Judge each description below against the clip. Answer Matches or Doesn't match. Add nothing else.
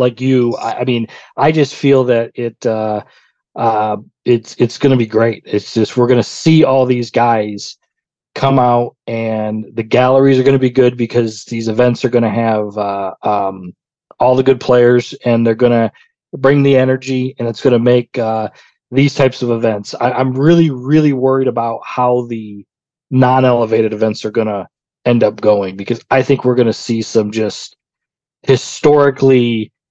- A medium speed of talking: Matches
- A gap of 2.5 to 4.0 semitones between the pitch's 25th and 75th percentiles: Matches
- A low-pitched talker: Matches